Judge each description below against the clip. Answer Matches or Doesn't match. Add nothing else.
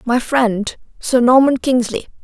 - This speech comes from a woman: Matches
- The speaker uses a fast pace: Doesn't match